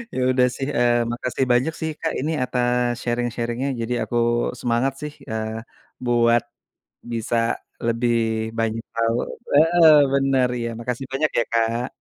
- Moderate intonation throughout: No, narrow, 2.3 semitones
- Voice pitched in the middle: No, low, 120 Hz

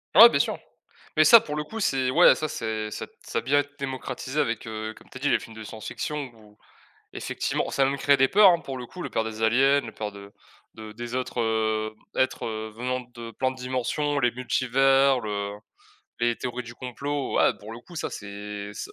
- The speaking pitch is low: Yes, low, 125 Hz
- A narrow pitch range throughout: No, average, 3.7 semitones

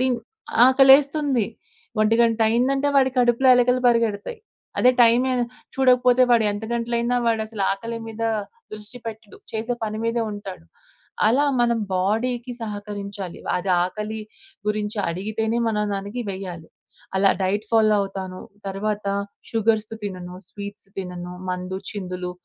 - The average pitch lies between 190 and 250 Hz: Yes, high, 220 Hz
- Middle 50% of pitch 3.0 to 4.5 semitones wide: Yes, average, 3.3 semitones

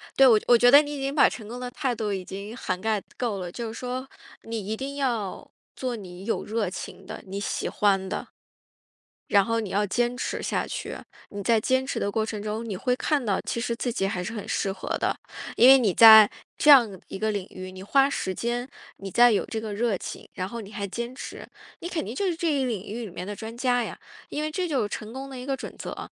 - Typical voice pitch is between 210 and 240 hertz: Yes, high, 230 Hz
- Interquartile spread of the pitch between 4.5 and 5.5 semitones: No, average, 3.9 semitones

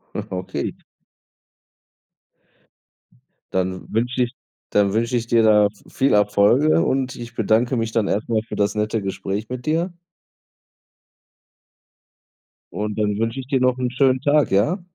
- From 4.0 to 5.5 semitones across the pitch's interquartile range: No, average, 3.6 semitones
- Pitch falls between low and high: No, low, 115 Hz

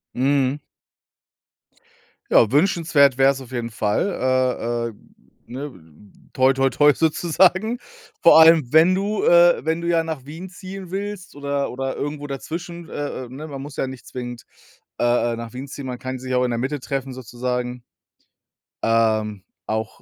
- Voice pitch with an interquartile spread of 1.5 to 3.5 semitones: No, average, 4.7 semitones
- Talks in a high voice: No, low, 135 Hz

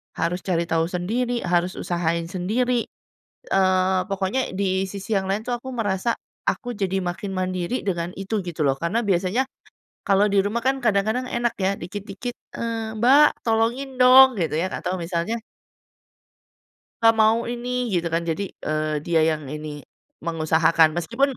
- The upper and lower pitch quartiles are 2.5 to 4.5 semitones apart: No, average, 5.1 semitones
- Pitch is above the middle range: Yes, high, 195 Hz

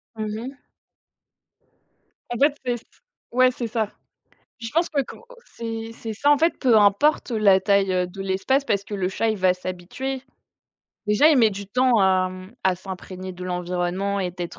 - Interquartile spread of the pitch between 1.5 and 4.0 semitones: No, average, 4.7 semitones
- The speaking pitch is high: Yes, high, 205 Hz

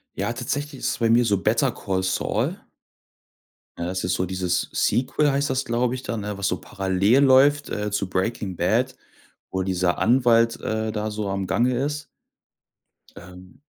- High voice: No, low, 110 Hz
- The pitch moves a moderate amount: Yes, average, 5.0 semitones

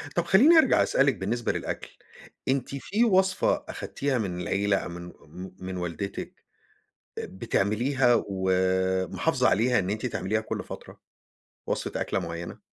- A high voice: No, low, 100 Hz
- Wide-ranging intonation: Yes, wide, 6.5 semitones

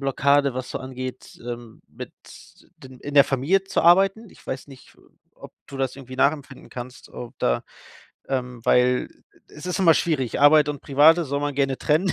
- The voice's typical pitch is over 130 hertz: Yes, medium, 140 Hz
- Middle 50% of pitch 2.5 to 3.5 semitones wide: Yes, average, 2.8 semitones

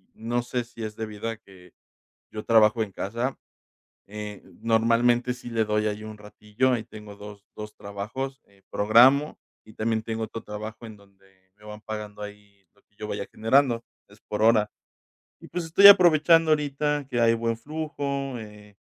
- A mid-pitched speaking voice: No, low, 110 Hz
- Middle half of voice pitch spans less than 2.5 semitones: No, average, 2.9 semitones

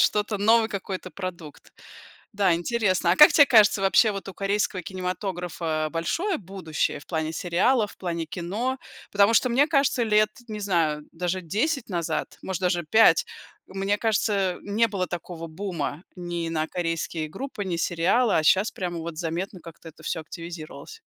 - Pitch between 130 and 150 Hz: No, medium, 185 Hz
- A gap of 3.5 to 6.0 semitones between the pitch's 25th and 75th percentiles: Yes, average, 3.9 semitones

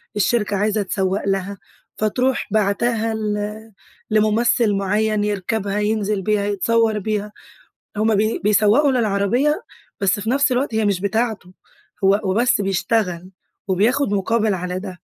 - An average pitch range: No, narrow, 2.0 semitones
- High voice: Yes, high, 210 Hz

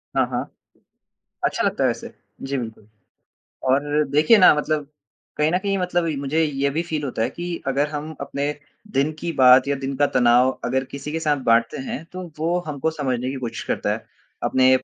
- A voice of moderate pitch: Yes, medium, 145 Hz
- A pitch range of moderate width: Yes, average, 3.3 semitones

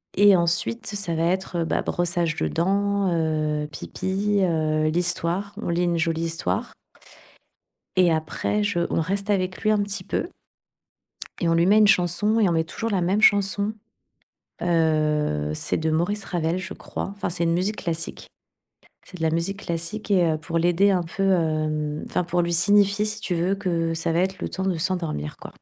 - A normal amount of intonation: Yes, average, 3.3 semitones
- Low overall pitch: No, medium, 175 Hz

